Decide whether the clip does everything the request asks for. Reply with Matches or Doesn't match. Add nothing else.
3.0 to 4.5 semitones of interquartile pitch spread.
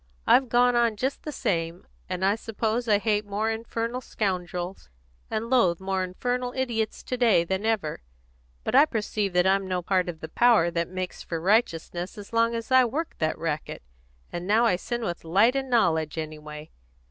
Doesn't match